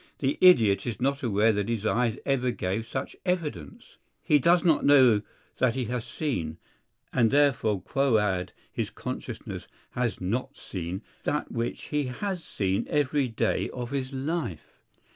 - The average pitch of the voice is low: Yes, low, 125 Hz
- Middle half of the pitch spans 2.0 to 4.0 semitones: No, average, 4.9 semitones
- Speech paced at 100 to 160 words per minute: Yes, average, 150 wpm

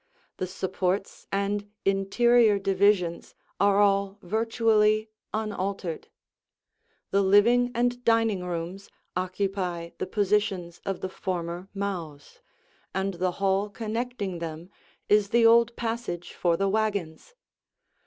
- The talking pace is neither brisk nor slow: No, slow, 110 wpm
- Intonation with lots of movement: No, average, 2.8 semitones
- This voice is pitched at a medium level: No, high, 195 Hz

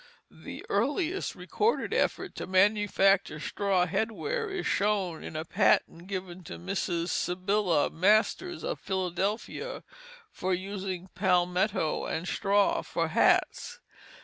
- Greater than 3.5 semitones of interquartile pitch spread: No, average, 2.8 semitones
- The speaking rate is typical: No, slow, 120 wpm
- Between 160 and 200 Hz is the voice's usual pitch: Yes, high, 190 Hz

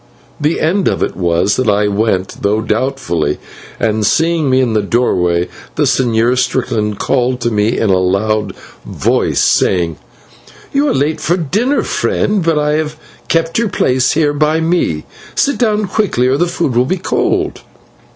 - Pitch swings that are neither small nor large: No, wide, 7.4 semitones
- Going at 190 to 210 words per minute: No, average, 170 wpm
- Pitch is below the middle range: Yes, low, 130 Hz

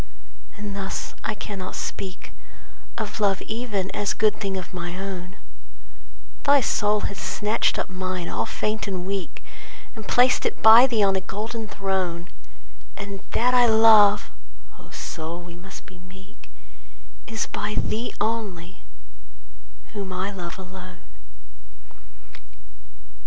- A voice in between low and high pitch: No, high, 195 Hz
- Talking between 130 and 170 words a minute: Yes, slow, 135 wpm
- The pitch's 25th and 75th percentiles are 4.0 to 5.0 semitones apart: No, average, 2.7 semitones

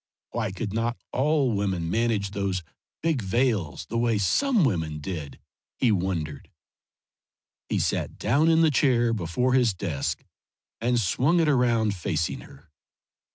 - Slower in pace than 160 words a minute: Yes, average, 140 wpm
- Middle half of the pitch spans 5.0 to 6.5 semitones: Yes, average, 5.3 semitones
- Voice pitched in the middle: No, low, 110 Hz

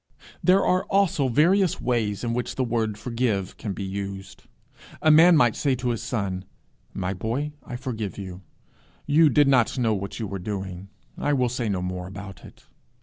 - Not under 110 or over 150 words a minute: No, average, 185 wpm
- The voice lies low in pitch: Yes, low, 115 Hz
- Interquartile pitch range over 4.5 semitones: Yes, average, 5.3 semitones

